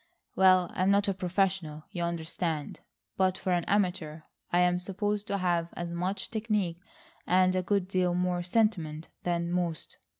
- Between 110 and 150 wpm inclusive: No, average, 160 wpm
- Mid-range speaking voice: Yes, medium, 180 Hz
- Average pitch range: No, narrow, 1.9 semitones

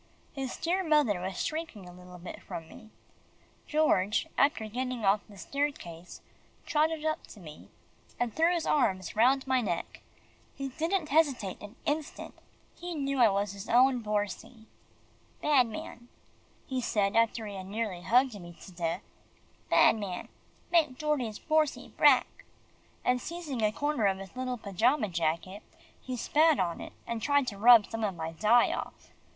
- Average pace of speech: Yes, average, 160 wpm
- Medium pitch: No, high, 230 Hz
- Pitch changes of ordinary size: No, wide, 6.4 semitones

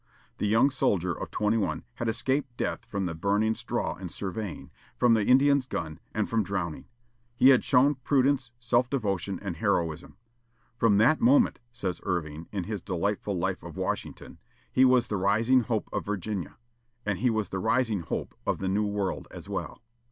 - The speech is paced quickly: No, average, 180 wpm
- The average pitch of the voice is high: No, low, 105 Hz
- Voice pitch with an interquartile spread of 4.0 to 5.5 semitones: Yes, average, 4.6 semitones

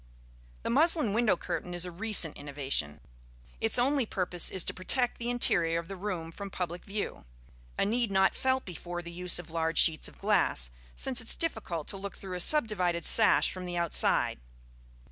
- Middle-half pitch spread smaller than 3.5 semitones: No, average, 4.8 semitones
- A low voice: No, medium, 185 Hz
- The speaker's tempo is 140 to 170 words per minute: No, average, 185 wpm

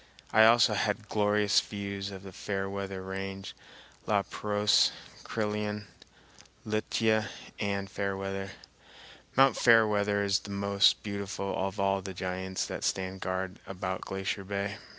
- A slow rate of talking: Yes, slow, 125 wpm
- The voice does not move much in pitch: Yes, narrow, 1.3 semitones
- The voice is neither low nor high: No, low, 100 Hz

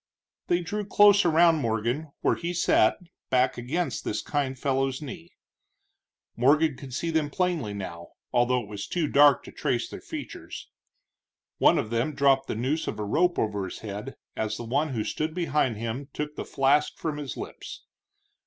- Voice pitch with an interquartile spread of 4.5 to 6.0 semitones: Yes, average, 5.3 semitones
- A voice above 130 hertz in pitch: Yes, medium, 140 Hz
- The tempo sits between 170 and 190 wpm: Yes, average, 175 wpm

